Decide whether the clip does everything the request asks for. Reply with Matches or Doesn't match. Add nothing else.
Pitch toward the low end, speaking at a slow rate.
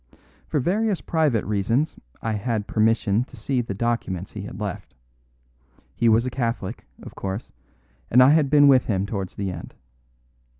Doesn't match